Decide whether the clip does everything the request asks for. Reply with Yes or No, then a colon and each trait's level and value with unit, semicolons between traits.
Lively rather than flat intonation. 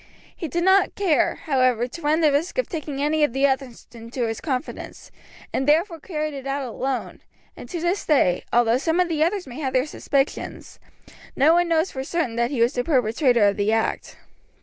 No: average, 4.7 semitones